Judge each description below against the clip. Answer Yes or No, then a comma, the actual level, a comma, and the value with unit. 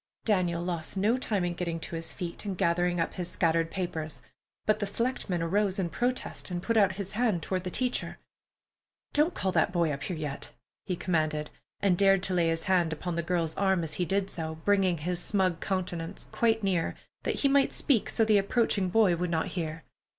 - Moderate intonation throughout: Yes, average, 3.1 semitones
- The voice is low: No, medium, 180 Hz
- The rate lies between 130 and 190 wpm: No, fast, 205 wpm